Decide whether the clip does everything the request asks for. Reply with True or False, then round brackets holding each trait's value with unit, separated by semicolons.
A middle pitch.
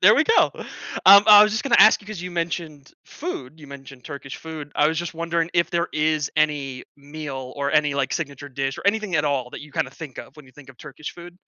True (150 Hz)